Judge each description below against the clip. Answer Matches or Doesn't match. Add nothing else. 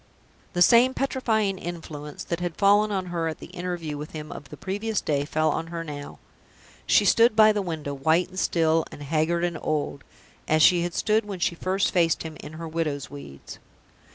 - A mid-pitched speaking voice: Matches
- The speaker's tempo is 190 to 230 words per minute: Matches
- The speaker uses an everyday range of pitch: Matches